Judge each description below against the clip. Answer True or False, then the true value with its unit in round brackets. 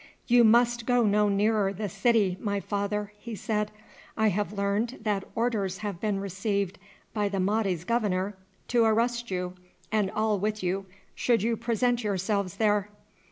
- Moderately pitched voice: False (210 Hz)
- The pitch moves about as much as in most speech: False (2.2 semitones)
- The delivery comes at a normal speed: True (160 wpm)